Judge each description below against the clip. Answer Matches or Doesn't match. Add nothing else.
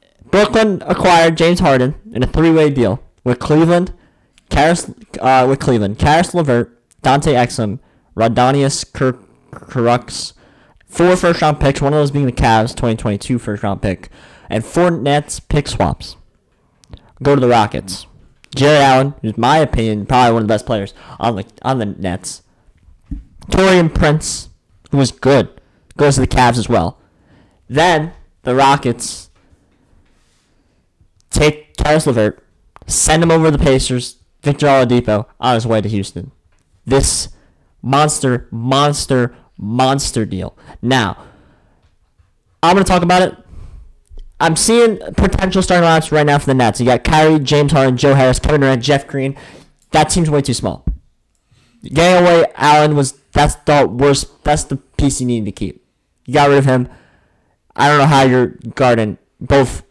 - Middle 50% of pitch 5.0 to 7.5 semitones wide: Matches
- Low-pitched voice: Matches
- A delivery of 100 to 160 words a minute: Matches